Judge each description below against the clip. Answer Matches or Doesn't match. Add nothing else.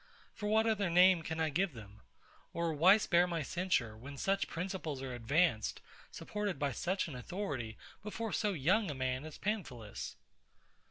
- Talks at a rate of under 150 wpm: Doesn't match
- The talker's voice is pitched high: Doesn't match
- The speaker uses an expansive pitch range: Matches